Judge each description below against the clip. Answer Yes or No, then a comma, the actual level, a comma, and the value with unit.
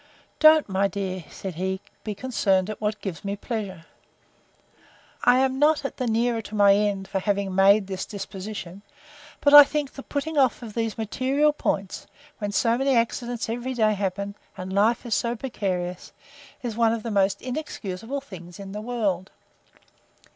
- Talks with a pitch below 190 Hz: No, high, 215 Hz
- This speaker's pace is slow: No, average, 160 wpm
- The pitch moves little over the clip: No, average, 4.1 semitones